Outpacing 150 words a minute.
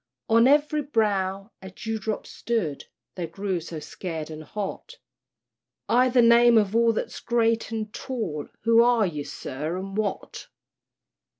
No: average, 140 wpm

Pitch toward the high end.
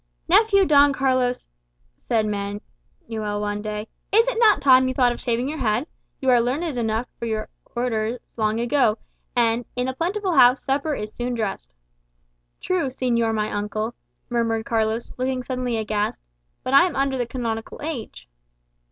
Yes: high, 245 Hz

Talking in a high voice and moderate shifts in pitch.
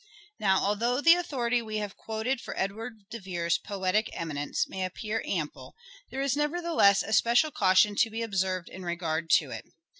Yes: high, 210 Hz; average, 4.2 semitones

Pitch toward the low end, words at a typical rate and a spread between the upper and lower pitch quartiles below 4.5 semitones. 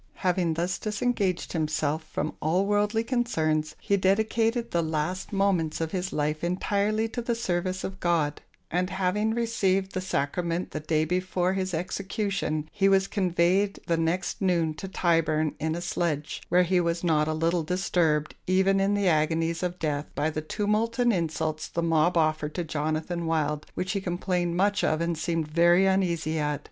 No: medium, 175 Hz; average, 175 wpm; average, 3.4 semitones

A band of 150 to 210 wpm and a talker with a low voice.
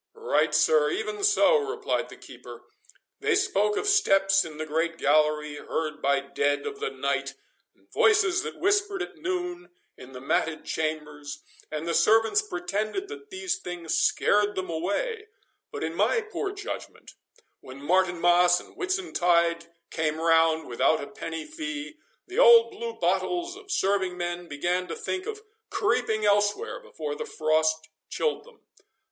No: average, 155 wpm; high, 205 Hz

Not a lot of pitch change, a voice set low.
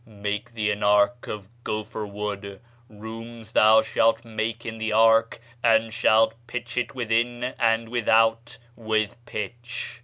Yes: narrow, 1.5 semitones; low, 110 Hz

